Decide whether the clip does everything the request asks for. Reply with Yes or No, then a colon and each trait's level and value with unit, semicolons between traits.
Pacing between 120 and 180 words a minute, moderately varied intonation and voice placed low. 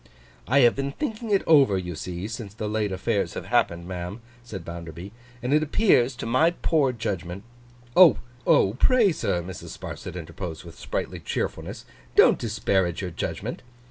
No: average, 160 wpm; wide, 7.4 semitones; low, 110 Hz